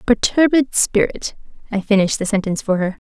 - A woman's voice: Yes, female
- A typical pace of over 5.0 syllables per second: Yes, 5.8 syllables/s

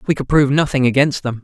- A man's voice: Yes, male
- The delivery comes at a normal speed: No, fast, 250 wpm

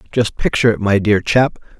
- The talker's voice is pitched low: Yes, low, 105 Hz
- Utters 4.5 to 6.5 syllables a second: Yes, 5.8 syllables/s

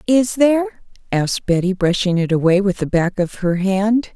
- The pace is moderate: Yes, average, 190 wpm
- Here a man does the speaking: No, female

